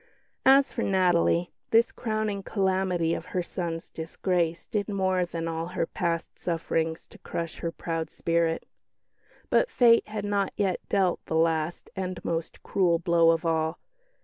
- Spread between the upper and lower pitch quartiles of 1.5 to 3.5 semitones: Yes, average, 2.8 semitones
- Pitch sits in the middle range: Yes, medium, 175 Hz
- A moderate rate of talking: Yes, average, 150 wpm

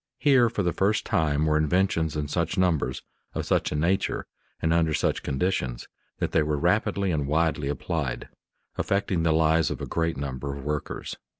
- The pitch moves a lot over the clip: No, average, 3.4 semitones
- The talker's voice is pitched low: Yes, very low, 80 Hz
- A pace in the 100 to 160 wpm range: No, average, 180 wpm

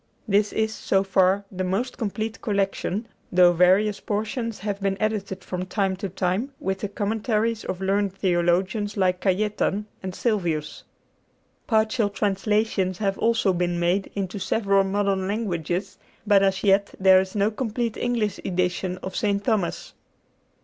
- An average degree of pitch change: No, narrow, 2.2 semitones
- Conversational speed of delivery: Yes, average, 145 wpm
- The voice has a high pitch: Yes, high, 200 Hz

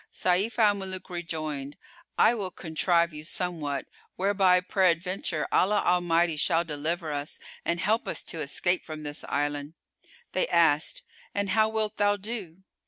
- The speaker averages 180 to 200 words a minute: No, average, 145 wpm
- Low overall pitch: No, medium, 175 Hz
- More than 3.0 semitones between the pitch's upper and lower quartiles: Yes, average, 3.7 semitones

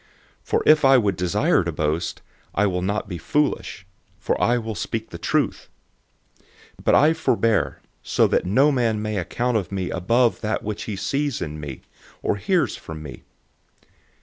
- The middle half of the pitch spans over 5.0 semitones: Yes, wide, 5.4 semitones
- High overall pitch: No, low, 105 Hz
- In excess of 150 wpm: Yes, average, 175 wpm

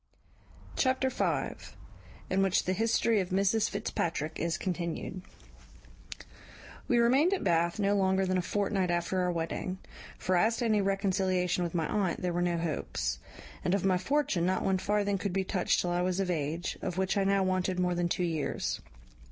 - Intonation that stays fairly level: Yes, narrow, 2.3 semitones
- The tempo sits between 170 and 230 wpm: Yes, average, 185 wpm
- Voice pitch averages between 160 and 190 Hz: Yes, medium, 185 Hz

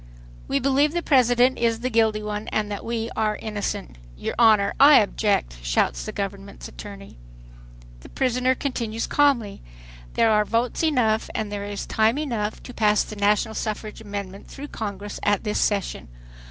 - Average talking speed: Yes, average, 165 wpm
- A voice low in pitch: No, high, 215 Hz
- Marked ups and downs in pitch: No, average, 2.9 semitones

